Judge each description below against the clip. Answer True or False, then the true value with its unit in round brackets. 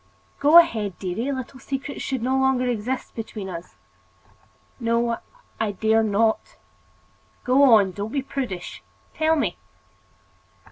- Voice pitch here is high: True (235 Hz)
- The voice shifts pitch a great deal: False (3.9 semitones)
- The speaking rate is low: True (125 wpm)